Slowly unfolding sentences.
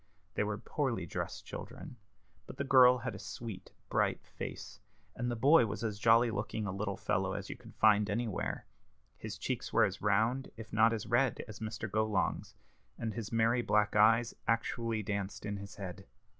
No: average, 185 wpm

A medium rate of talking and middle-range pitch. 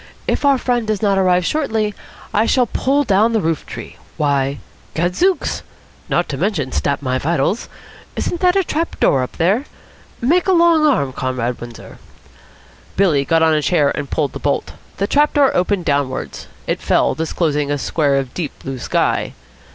Yes: average, 175 wpm; medium, 180 Hz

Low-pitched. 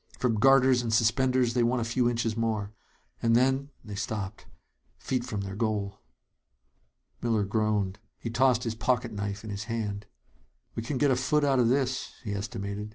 Yes: low, 115 Hz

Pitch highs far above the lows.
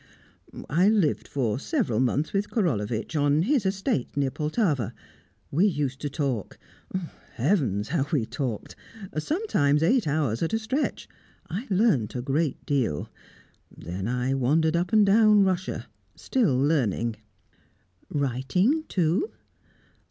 Yes: wide, 7.4 semitones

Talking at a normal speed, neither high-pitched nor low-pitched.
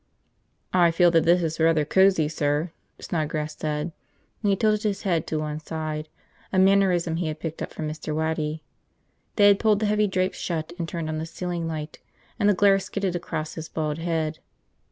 Yes: average, 195 wpm; medium, 165 Hz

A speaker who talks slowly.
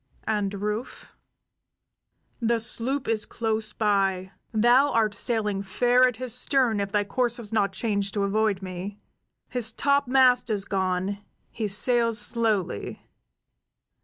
Yes: slow, 130 wpm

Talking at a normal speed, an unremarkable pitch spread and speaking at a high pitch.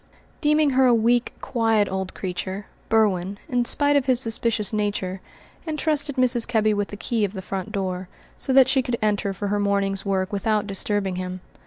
Yes: average, 185 wpm; average, 3.9 semitones; high, 210 Hz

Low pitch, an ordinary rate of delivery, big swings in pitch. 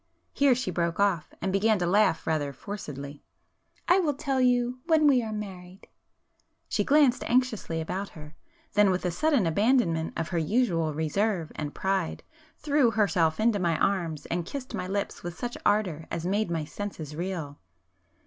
No: high, 195 Hz; average, 165 wpm; wide, 6.5 semitones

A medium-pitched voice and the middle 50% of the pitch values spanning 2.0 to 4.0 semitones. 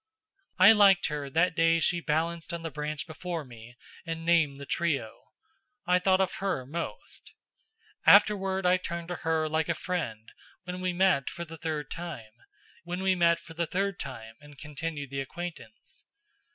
Yes: medium, 165 Hz; average, 3.3 semitones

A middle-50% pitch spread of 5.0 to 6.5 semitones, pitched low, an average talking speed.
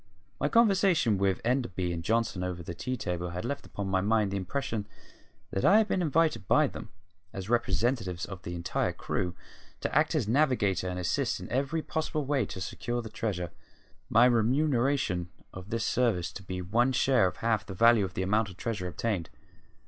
Yes: wide, 5.6 semitones; low, 110 Hz; average, 190 wpm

